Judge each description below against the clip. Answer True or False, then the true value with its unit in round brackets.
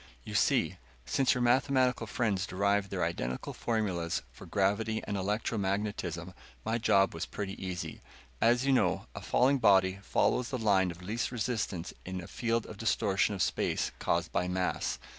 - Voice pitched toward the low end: True (100 Hz)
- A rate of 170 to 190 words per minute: False (160 wpm)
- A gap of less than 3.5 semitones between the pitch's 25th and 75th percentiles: False (3.8 semitones)